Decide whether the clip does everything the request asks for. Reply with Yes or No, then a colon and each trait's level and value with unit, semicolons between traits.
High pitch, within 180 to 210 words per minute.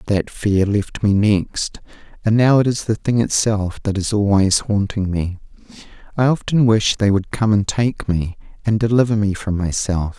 No: low, 105 Hz; average, 185 wpm